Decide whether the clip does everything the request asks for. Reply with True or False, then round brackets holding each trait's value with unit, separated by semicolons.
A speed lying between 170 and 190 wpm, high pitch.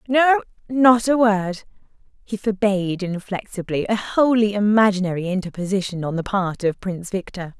False (135 wpm; 200 Hz)